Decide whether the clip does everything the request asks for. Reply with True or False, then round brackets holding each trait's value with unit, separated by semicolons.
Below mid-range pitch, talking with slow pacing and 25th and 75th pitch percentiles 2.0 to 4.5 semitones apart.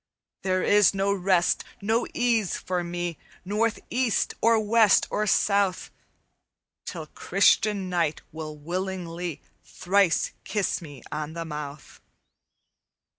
False (185 Hz; 115 wpm; 3.7 semitones)